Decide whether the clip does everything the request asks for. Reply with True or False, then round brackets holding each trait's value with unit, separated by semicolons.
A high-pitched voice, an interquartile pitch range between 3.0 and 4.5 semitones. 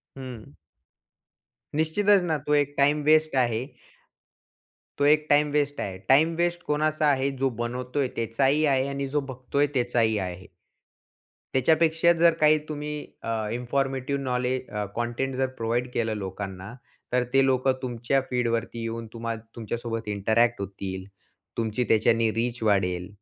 False (125 Hz; 4.2 semitones)